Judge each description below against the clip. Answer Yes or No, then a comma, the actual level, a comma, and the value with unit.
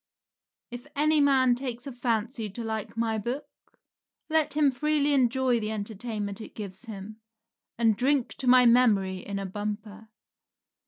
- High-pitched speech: Yes, high, 235 Hz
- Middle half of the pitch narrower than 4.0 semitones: Yes, average, 3.6 semitones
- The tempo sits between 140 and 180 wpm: Yes, average, 150 wpm